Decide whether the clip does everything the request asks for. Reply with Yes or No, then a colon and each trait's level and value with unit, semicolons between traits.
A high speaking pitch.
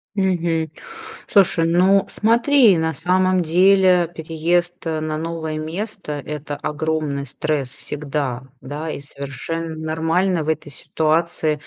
No: medium, 160 Hz